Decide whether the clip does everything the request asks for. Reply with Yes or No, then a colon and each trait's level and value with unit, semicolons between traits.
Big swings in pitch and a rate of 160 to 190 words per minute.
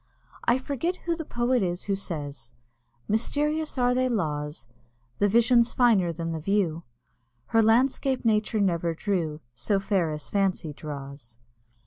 No: wide, 7.2 semitones; average, 140 wpm